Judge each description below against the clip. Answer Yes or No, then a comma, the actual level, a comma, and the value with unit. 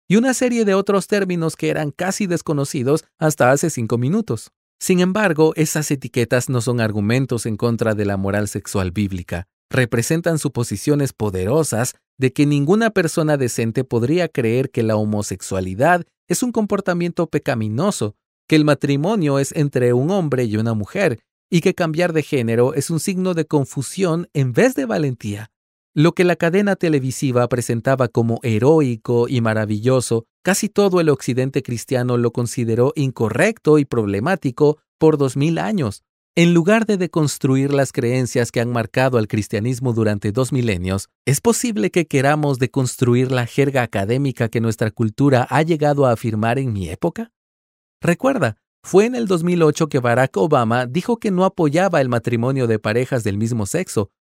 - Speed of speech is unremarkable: Yes, average, 160 wpm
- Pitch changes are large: Yes, wide, 6.0 semitones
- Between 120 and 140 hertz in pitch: Yes, low, 135 Hz